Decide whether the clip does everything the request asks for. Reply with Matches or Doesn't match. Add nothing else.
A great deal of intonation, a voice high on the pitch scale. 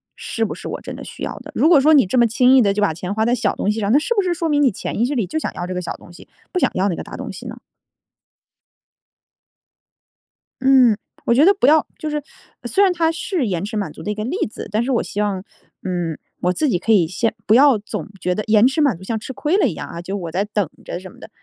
Matches